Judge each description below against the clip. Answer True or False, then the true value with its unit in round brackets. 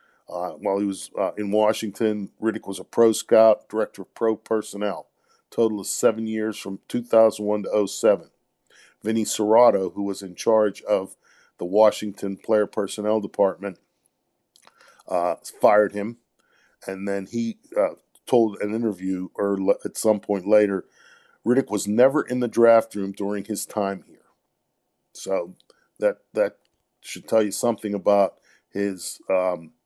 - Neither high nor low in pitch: False (105 Hz)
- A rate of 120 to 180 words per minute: True (145 wpm)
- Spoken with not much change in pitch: True (2.0 semitones)